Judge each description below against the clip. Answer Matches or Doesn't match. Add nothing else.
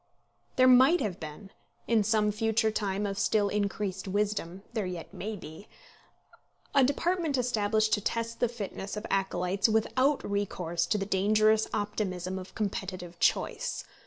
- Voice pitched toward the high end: Matches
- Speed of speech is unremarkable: Matches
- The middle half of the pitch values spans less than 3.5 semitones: Matches